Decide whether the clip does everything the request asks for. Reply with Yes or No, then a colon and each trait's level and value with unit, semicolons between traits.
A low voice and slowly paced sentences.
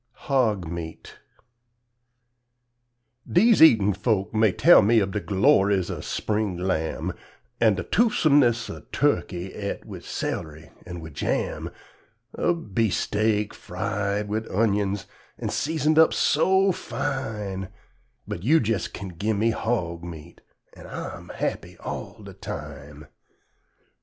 Yes: low, 105 Hz; slow, 120 wpm